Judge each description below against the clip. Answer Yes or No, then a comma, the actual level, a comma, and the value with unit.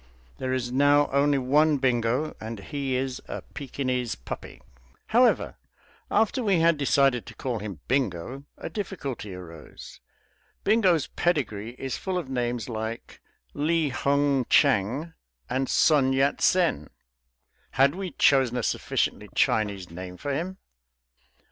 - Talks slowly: Yes, slow, 130 wpm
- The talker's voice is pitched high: No, low, 135 Hz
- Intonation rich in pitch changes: No, average, 4.2 semitones